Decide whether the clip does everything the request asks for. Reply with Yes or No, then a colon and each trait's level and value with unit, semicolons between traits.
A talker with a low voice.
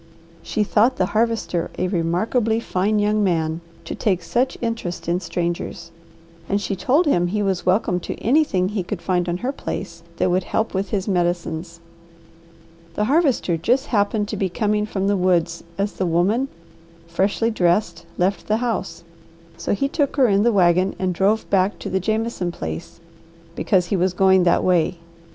No: high, 190 Hz